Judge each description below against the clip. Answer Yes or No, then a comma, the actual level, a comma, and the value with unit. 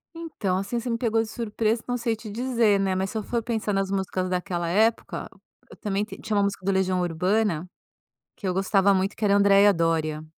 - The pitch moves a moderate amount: Yes, average, 3.0 semitones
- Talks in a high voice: Yes, high, 200 Hz